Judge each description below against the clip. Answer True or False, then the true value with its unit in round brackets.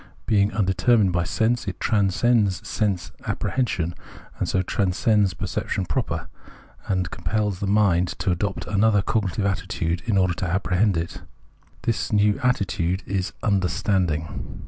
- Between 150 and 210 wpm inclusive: False (135 wpm)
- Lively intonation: False (2.8 semitones)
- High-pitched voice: False (95 Hz)